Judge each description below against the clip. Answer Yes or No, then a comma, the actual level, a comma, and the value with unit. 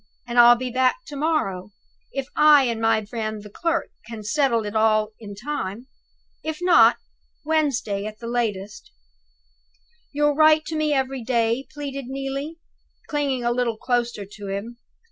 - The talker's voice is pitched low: No, high, 240 Hz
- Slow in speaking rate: No, average, 155 wpm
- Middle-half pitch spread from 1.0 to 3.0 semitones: No, average, 5.0 semitones